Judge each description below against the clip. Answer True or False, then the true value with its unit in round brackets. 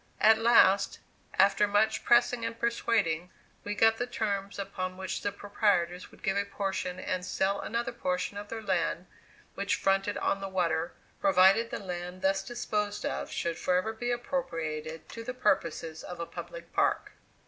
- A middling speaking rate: True (165 wpm)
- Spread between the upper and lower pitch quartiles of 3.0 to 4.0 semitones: True (3.4 semitones)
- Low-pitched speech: False (195 Hz)